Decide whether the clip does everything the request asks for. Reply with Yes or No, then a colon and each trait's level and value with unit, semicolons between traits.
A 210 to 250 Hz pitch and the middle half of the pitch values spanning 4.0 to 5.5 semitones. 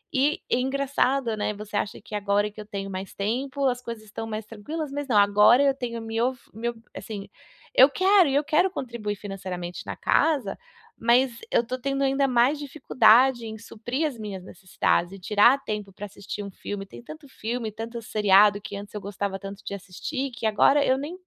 Yes: high, 225 Hz; average, 4.6 semitones